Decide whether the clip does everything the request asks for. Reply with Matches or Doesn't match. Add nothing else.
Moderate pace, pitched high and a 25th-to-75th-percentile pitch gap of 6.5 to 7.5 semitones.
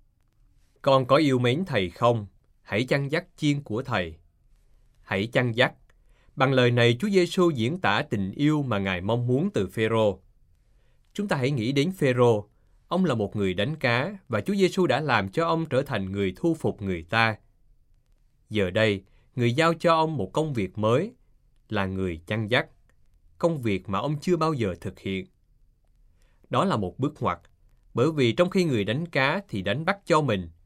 Doesn't match